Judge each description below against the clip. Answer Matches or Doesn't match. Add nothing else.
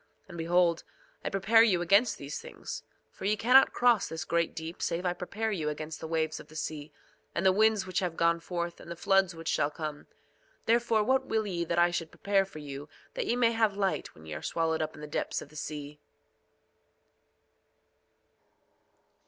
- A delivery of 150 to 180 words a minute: Doesn't match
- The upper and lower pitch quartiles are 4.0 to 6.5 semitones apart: Matches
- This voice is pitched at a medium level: Matches